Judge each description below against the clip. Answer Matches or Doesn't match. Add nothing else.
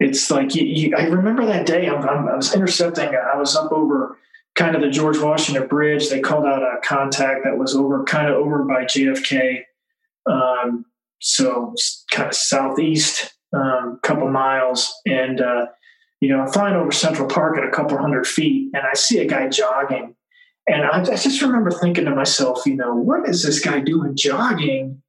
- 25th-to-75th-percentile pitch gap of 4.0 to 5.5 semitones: Matches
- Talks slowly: Doesn't match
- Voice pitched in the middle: Matches